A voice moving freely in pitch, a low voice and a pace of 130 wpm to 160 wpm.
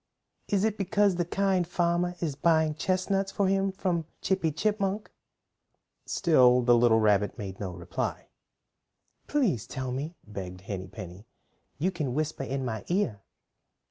No: wide, 8.7 semitones; medium, 160 Hz; average, 140 wpm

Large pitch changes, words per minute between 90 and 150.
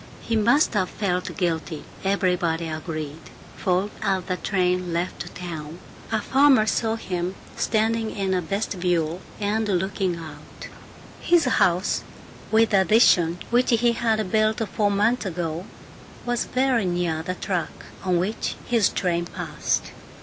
No: average, 4.0 semitones; slow, 135 wpm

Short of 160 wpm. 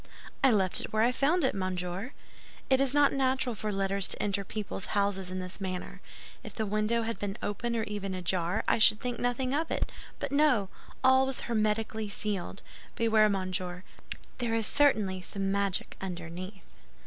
No: average, 170 wpm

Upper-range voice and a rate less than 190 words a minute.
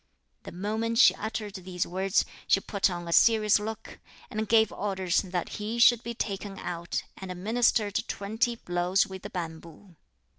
Yes: high, 200 Hz; average, 160 wpm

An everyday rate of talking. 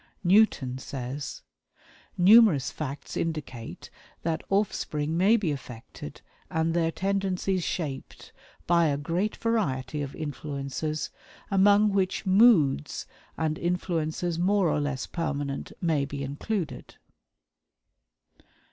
No: slow, 105 wpm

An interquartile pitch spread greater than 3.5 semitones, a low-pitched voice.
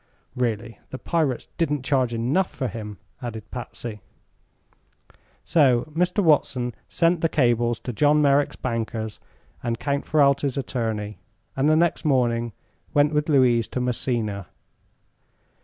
Yes: average, 3.9 semitones; low, 125 Hz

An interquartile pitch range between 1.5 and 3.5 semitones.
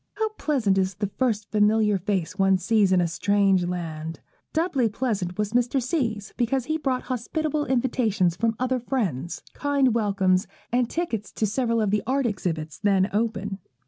No: average, 4.8 semitones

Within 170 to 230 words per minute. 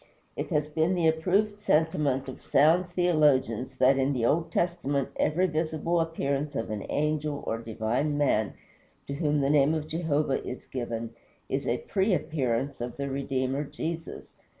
No: average, 160 wpm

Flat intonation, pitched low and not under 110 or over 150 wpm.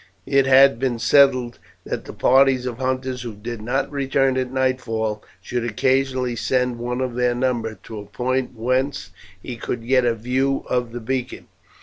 No: narrow, 1.8 semitones; low, 125 Hz; average, 175 wpm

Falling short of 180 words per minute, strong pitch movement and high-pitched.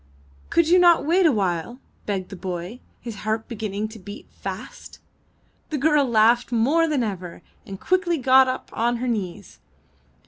Yes: average, 165 wpm; wide, 6.2 semitones; high, 235 Hz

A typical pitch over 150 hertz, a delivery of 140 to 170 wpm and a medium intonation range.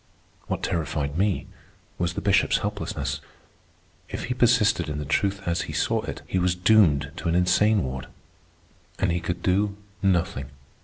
No: very low, 90 Hz; average, 160 wpm; average, 3.7 semitones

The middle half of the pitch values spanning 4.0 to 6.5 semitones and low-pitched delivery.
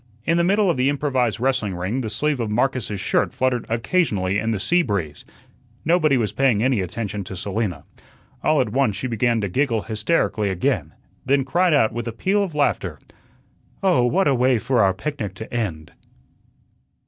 Yes: average, 5.3 semitones; low, 120 Hz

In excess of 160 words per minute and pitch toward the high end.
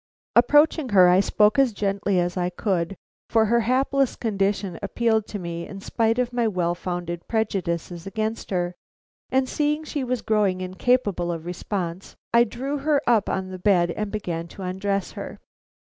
Yes: average, 170 wpm; high, 200 Hz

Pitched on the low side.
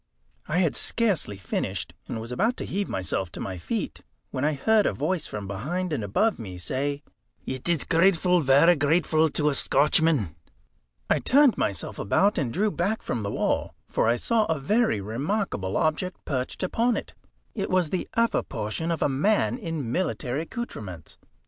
No: medium, 155 Hz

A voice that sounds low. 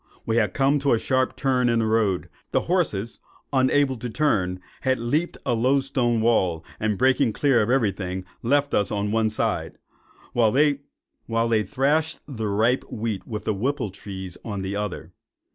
Yes: low, 115 Hz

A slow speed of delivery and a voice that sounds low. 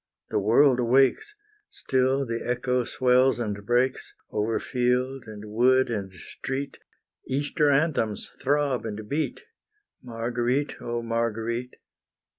Yes: slow, 110 wpm; low, 125 Hz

